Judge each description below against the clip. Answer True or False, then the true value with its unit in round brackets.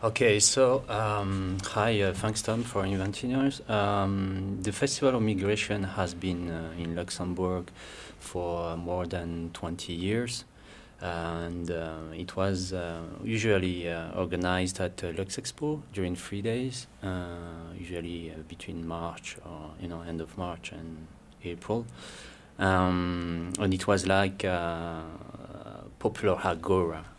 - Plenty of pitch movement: False (3.3 semitones)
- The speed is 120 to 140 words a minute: True (135 wpm)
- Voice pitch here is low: True (90 Hz)